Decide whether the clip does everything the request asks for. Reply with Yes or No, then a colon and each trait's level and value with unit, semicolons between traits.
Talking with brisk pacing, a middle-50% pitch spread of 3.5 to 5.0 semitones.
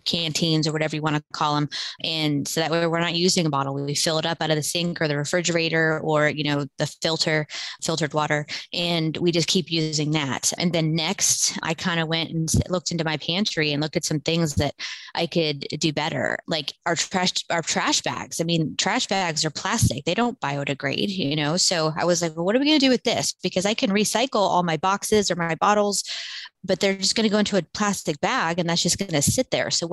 No: fast, 245 wpm; average, 3.0 semitones